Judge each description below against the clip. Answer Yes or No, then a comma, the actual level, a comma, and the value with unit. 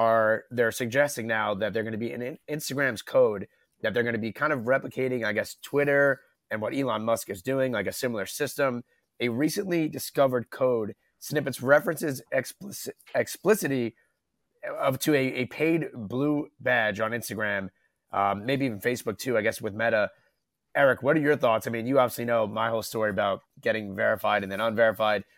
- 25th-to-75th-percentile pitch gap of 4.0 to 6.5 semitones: Yes, average, 4.3 semitones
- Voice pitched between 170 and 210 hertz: No, low, 125 Hz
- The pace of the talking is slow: No, average, 185 wpm